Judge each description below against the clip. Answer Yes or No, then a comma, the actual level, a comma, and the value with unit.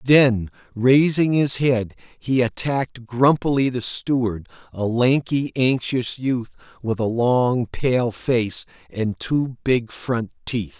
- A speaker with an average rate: No, slow, 130 wpm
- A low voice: Yes, low, 125 Hz